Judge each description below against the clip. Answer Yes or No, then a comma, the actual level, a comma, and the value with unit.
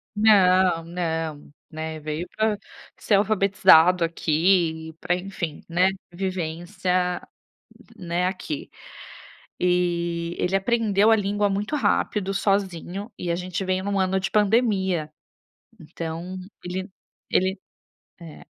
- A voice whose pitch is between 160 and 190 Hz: Yes, medium, 185 Hz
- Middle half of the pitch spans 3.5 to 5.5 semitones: No, average, 2.7 semitones